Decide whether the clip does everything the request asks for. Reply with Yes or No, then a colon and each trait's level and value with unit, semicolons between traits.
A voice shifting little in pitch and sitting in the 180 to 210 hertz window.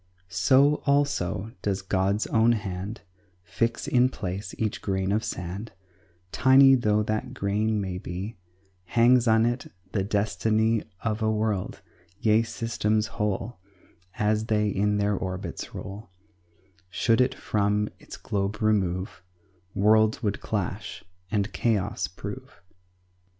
No: narrow, 2.3 semitones; low, 105 Hz